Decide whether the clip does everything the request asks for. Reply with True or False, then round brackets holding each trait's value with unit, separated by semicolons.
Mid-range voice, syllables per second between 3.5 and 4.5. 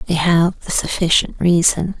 True (170 Hz; 4.4 syllables/s)